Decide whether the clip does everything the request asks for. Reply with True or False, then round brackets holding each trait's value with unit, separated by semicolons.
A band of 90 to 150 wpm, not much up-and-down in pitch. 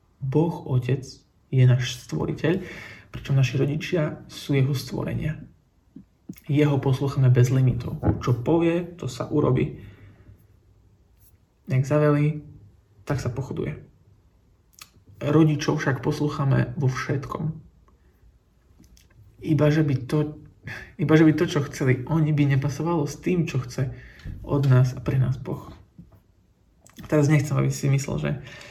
False (115 wpm; 3.7 semitones)